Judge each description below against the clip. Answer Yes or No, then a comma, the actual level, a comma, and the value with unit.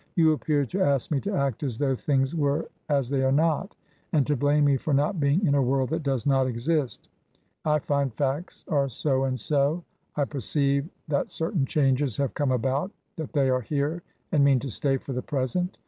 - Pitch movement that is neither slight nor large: No, narrow, 2.2 semitones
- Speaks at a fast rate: Yes, fast, 215 wpm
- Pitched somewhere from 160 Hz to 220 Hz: No, medium, 140 Hz